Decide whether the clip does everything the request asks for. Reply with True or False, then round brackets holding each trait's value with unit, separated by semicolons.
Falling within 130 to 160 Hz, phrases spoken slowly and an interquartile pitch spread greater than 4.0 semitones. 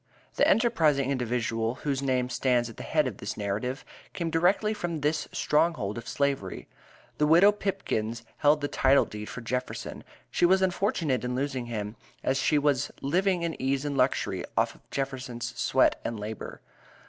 False (135 Hz; 170 wpm; 4.8 semitones)